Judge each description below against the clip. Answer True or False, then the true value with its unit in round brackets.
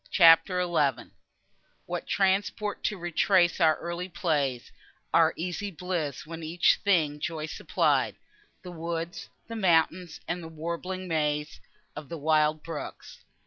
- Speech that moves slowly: True (130 wpm)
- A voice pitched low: False (165 Hz)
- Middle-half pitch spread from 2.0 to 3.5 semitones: True (2.6 semitones)